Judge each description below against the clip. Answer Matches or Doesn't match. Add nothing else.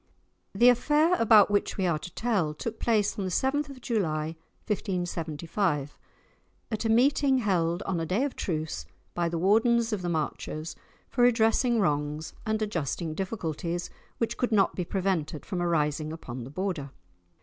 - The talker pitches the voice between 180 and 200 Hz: Matches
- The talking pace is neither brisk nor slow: Matches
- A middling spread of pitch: Doesn't match